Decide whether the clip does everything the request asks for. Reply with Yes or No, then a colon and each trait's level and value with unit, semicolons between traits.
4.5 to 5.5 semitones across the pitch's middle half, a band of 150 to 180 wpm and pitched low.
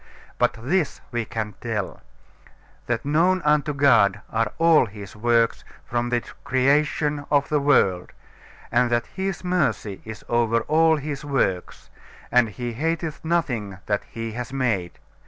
No: average, 5.0 semitones; average, 140 wpm; low, 125 Hz